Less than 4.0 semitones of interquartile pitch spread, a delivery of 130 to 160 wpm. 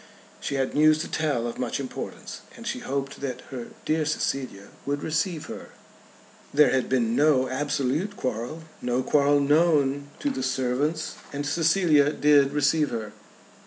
Yes: average, 2.9 semitones; average, 155 wpm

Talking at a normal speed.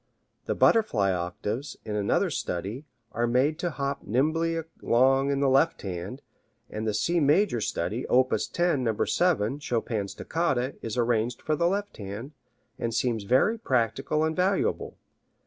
Yes: average, 150 wpm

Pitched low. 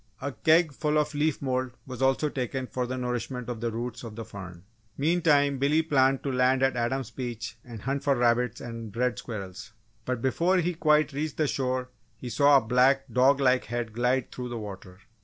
Yes: low, 130 Hz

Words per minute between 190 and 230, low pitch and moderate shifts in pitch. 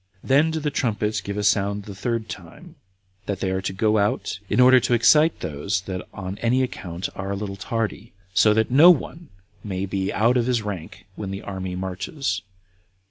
Yes: average, 195 wpm; low, 105 Hz; average, 4.0 semitones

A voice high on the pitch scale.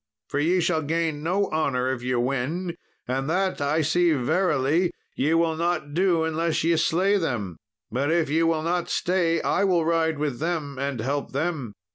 No: medium, 160 Hz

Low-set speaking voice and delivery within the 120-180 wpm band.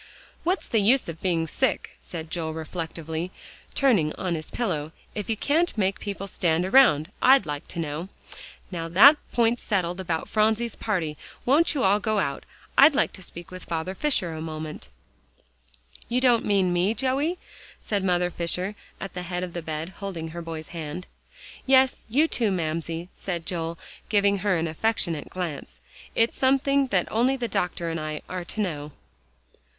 No: medium, 185 Hz; average, 170 wpm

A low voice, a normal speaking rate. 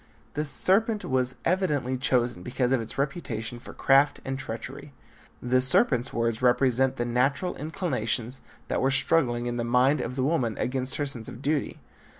Yes: low, 130 Hz; average, 165 wpm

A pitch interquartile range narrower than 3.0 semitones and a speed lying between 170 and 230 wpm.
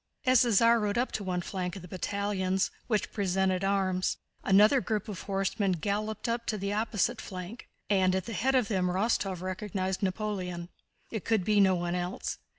Yes: narrow, 2.5 semitones; average, 185 wpm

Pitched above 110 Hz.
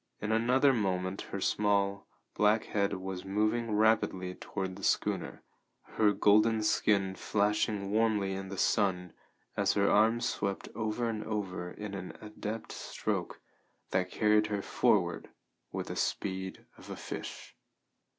No: low, 105 Hz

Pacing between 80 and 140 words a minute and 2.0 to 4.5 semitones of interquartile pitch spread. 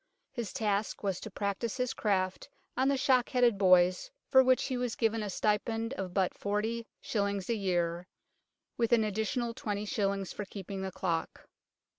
No: average, 160 wpm; average, 3.3 semitones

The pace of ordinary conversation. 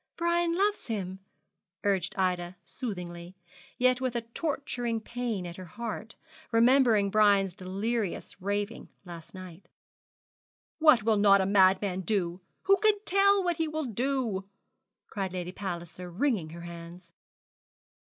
No: slow, 130 wpm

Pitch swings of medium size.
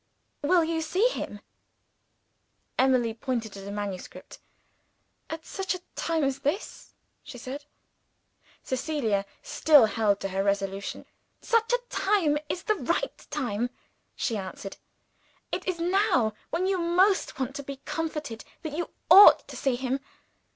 No: wide, 7.3 semitones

